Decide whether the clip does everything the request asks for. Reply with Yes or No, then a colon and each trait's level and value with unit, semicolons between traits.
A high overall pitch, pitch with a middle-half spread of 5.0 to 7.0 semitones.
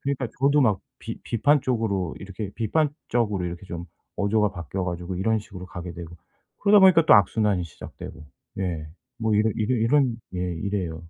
No: low, 105 Hz; average, 5.3 semitones